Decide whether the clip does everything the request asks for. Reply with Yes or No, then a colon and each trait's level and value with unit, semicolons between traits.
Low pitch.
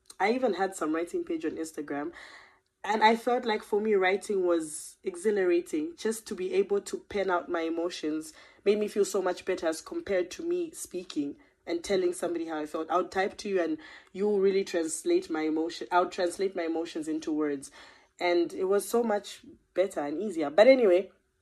No: high, 190 Hz